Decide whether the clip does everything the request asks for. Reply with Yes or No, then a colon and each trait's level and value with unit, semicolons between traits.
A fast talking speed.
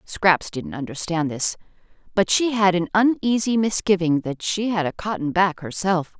No: average, 165 wpm